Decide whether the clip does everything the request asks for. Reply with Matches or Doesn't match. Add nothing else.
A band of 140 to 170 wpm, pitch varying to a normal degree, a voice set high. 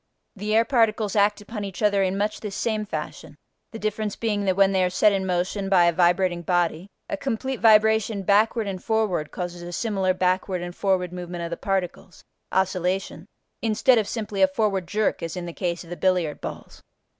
Doesn't match